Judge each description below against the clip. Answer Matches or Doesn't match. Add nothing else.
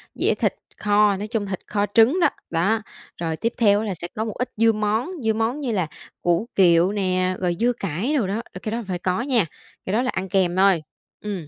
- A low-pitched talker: Doesn't match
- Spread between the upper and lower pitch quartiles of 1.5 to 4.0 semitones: Matches